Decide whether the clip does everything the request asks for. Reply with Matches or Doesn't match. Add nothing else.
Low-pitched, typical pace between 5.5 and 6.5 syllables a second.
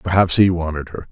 Matches